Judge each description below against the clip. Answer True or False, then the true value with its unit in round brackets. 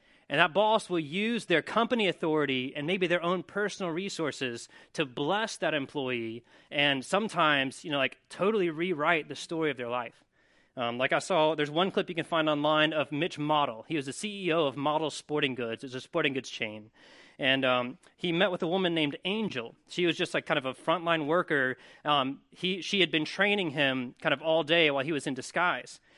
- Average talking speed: False (210 wpm)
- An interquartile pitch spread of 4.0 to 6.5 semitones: True (4.5 semitones)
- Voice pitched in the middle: True (155 Hz)